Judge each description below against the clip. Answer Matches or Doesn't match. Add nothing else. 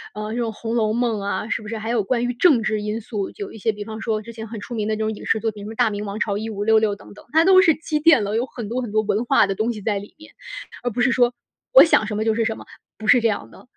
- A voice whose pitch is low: Doesn't match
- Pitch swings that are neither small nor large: Doesn't match